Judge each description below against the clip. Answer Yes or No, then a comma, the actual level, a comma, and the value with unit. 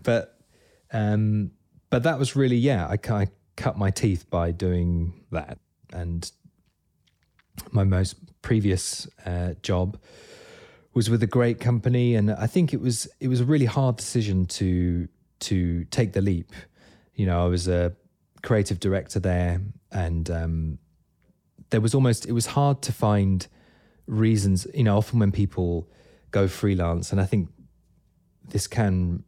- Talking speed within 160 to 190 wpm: No, average, 150 wpm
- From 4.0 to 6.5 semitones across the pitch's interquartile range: Yes, average, 4.9 semitones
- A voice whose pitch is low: Yes, low, 100 Hz